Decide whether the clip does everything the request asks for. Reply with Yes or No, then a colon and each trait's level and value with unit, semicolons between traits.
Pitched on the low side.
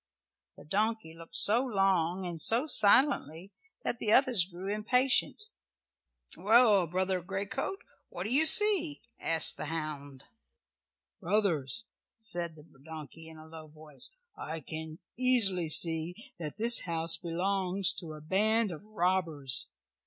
No: medium, 185 Hz